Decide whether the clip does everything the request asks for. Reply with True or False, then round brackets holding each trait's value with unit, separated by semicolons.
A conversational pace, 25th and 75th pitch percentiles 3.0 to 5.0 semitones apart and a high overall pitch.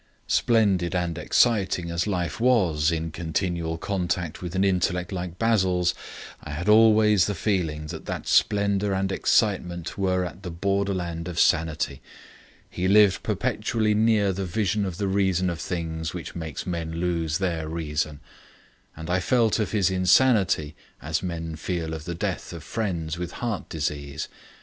False (155 wpm; 3.3 semitones; 90 Hz)